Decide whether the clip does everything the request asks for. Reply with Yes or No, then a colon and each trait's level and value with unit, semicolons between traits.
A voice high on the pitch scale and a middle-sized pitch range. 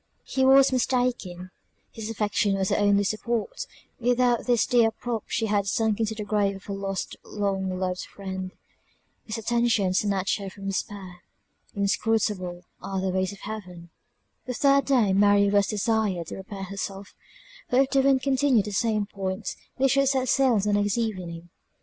Yes: high, 205 Hz; average, 3.5 semitones